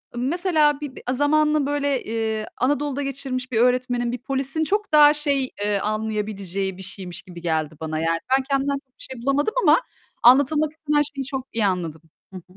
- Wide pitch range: Yes, wide, 5.7 semitones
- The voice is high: Yes, very high, 260 Hz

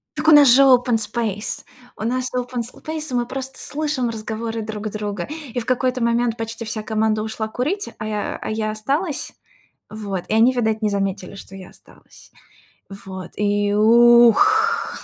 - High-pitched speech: Yes, high, 230 Hz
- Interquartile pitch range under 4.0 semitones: Yes, average, 3.0 semitones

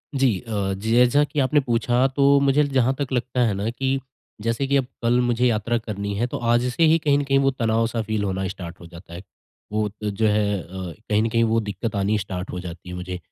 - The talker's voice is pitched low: Yes, low, 115 Hz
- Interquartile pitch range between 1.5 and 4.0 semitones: No, average, 4.5 semitones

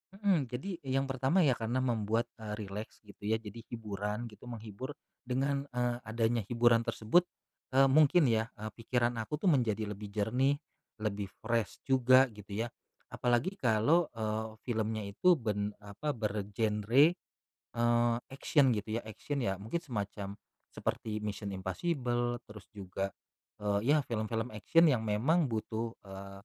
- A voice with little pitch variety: No, average, 3.5 semitones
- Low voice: Yes, low, 115 Hz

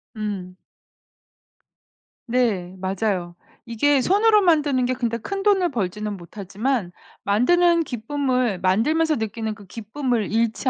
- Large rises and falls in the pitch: Yes, wide, 6.0 semitones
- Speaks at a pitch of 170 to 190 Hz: No, high, 230 Hz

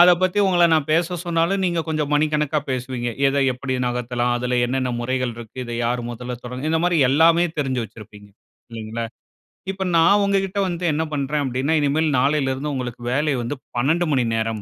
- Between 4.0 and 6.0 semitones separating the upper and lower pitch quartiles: Yes, average, 4.9 semitones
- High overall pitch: No, medium, 140 Hz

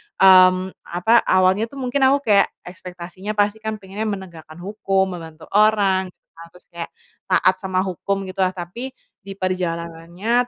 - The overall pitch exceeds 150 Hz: Yes, high, 190 Hz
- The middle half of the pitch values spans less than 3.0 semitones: Yes, narrow, 2.6 semitones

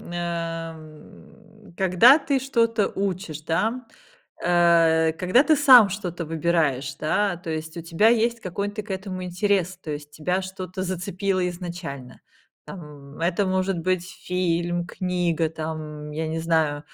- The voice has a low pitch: No, medium, 175 Hz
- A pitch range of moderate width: Yes, average, 3.2 semitones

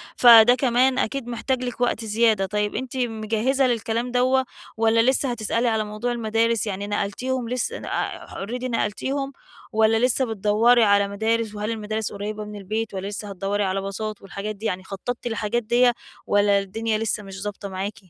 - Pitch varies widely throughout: No, average, 2.9 semitones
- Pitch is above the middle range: Yes, high, 220 Hz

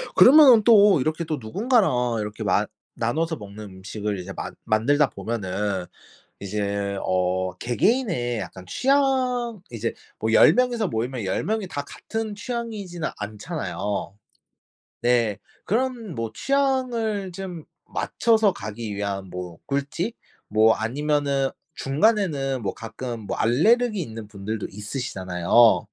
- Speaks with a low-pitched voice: Yes, low, 130 Hz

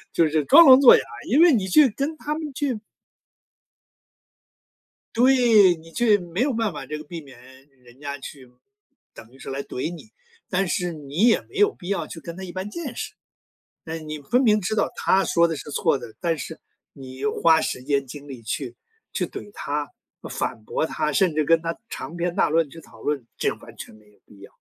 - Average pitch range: No, wide, 6.8 semitones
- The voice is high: No, medium, 165 Hz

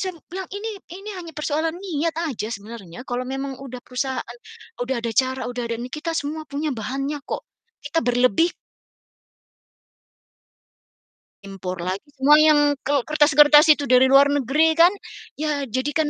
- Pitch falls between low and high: No, very high, 285 Hz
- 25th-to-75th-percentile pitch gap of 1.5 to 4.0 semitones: Yes, average, 3.7 semitones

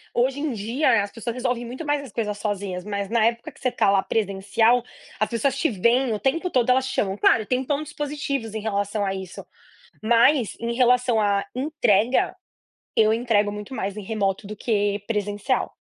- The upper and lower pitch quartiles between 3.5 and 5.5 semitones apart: Yes, average, 3.8 semitones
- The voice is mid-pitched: No, high, 230 Hz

